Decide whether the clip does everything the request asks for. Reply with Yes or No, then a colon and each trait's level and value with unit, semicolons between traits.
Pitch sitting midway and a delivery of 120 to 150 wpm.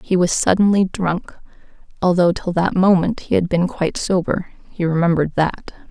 No: medium, 180 Hz; average, 160 wpm